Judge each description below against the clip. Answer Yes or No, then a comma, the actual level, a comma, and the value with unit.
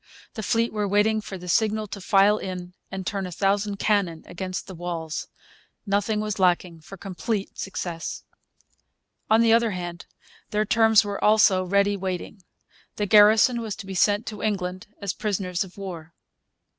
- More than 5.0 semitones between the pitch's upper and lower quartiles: No, average, 2.7 semitones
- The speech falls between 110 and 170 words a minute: Yes, average, 165 wpm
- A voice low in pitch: No, high, 200 Hz